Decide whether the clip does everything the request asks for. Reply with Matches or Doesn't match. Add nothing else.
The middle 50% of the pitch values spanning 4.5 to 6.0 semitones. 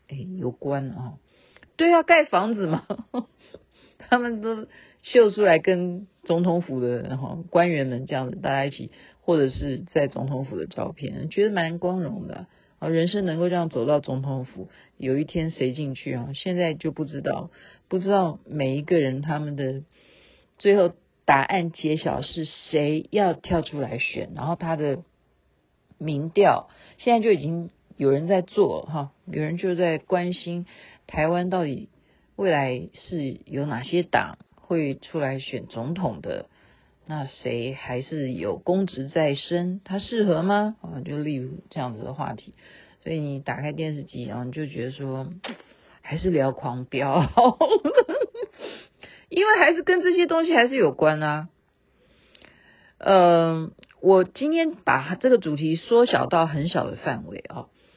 Matches